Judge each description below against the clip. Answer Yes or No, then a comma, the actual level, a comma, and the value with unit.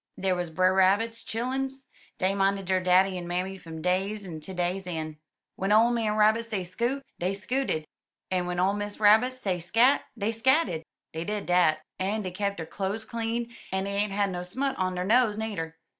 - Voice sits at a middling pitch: No, high, 195 Hz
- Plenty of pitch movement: No, average, 3.6 semitones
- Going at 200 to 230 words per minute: Yes, fast, 205 wpm